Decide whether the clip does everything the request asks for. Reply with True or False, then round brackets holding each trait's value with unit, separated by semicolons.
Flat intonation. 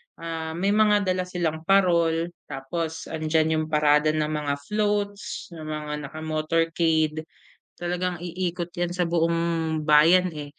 True (2.2 semitones)